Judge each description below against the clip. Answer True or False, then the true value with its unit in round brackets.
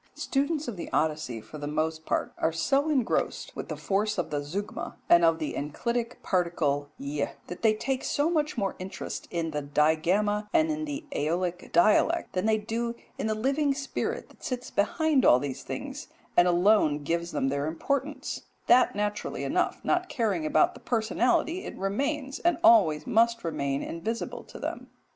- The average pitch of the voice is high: True (205 Hz)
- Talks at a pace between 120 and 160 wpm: False (175 wpm)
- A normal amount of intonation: False (8.7 semitones)